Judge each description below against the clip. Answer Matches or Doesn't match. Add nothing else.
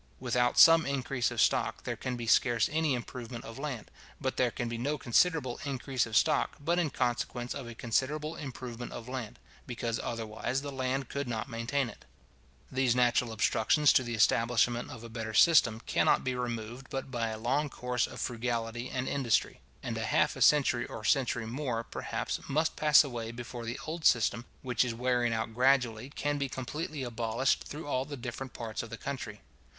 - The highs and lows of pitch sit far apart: Doesn't match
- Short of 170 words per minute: Doesn't match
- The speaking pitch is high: Doesn't match